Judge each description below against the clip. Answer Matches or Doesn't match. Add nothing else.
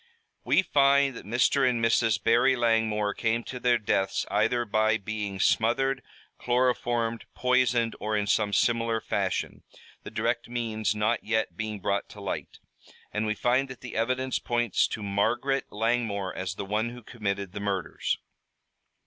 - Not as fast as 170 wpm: Matches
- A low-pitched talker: Matches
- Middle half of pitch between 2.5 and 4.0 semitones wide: Matches